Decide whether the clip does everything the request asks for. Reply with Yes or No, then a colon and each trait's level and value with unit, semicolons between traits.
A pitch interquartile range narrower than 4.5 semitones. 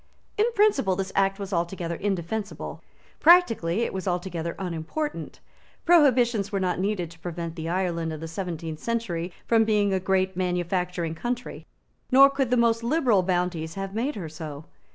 No: average, 5.2 semitones